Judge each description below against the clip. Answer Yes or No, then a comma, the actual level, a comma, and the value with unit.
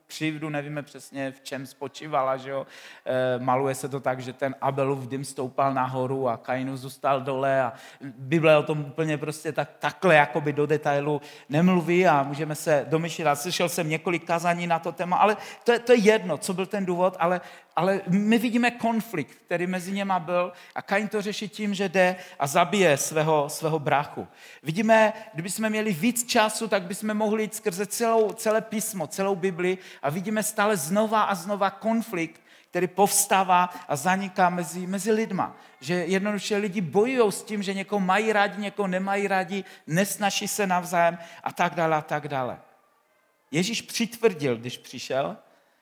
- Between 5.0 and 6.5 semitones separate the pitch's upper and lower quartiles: Yes, wide, 5.5 semitones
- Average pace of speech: No, fast, 175 wpm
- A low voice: No, medium, 180 Hz